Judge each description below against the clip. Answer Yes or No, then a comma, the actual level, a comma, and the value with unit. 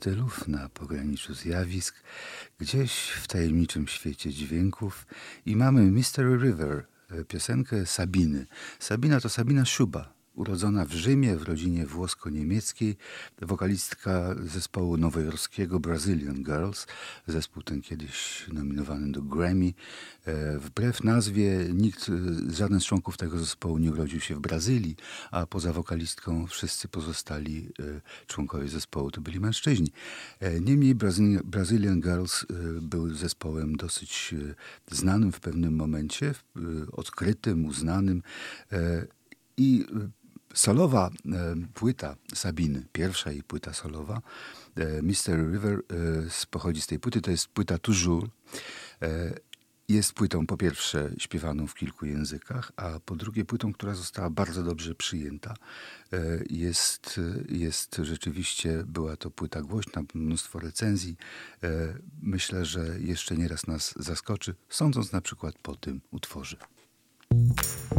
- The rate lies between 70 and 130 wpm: Yes, average, 115 wpm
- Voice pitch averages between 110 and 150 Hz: No, very low, 85 Hz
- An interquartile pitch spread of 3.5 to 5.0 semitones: Yes, average, 4.2 semitones